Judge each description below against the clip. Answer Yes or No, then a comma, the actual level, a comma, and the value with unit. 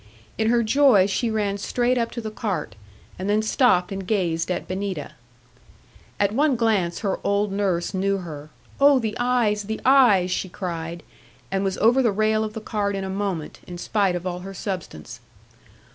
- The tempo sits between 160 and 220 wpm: Yes, average, 185 wpm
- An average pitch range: Yes, average, 3.2 semitones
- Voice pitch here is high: Yes, high, 200 Hz